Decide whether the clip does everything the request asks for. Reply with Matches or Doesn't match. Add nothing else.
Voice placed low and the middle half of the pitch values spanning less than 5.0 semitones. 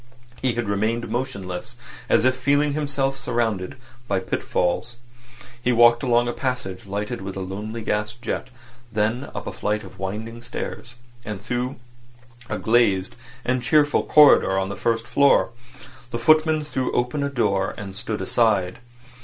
Matches